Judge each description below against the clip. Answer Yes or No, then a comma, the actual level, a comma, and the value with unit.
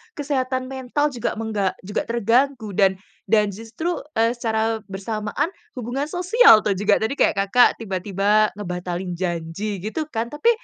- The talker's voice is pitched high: Yes, high, 220 Hz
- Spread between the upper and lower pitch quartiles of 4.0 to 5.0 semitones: Yes, average, 4.6 semitones